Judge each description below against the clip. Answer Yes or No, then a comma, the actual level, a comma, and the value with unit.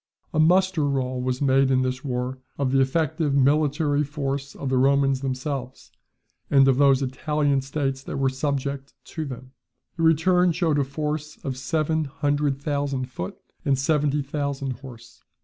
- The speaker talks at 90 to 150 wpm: No, average, 160 wpm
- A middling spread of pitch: No, narrow, 2.1 semitones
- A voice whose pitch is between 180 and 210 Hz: No, medium, 140 Hz